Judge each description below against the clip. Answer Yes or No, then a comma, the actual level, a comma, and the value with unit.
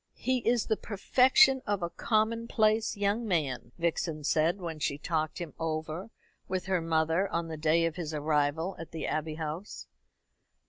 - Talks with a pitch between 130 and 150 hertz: No, medium, 170 Hz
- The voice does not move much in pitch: No, average, 4.7 semitones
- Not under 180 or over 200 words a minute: No, average, 165 wpm